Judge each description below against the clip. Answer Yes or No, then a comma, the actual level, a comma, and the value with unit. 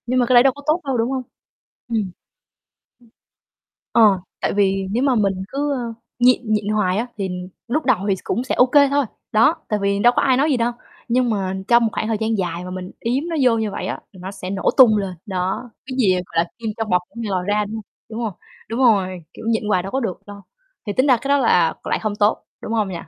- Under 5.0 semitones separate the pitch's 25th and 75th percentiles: Yes, average, 4.3 semitones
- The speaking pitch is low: No, high, 220 Hz